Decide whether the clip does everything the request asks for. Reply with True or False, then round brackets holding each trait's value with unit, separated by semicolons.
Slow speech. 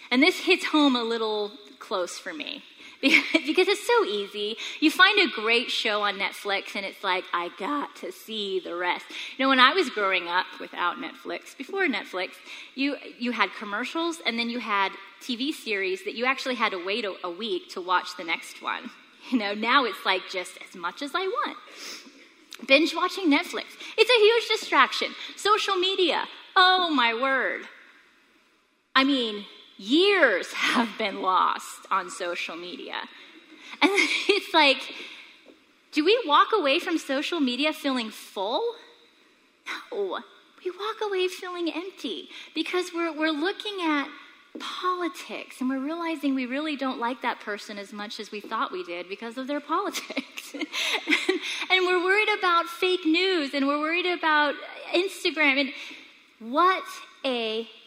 False (160 wpm)